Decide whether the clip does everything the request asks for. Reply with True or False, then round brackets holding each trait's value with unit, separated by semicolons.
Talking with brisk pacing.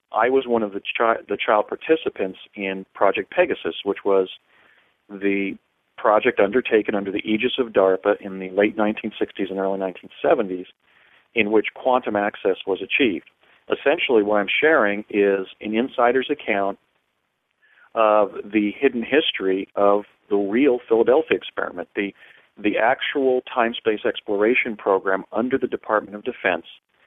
False (140 wpm)